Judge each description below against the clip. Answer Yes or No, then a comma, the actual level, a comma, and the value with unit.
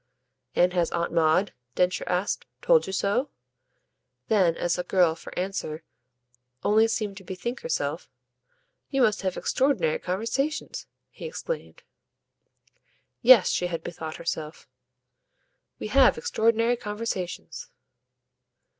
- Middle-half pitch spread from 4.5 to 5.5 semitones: Yes, average, 4.8 semitones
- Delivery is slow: Yes, slow, 115 wpm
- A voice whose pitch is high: Yes, high, 195 Hz